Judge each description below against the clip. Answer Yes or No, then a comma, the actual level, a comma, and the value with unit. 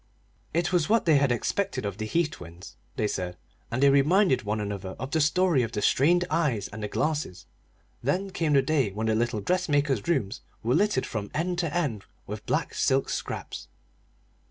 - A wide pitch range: Yes, wide, 7.6 semitones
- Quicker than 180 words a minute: Yes, average, 190 wpm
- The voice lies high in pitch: No, low, 135 Hz